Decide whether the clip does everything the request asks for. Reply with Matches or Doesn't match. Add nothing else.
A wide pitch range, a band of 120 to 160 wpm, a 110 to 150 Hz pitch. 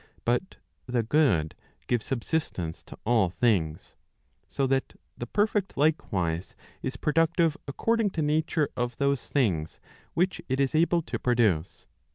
Matches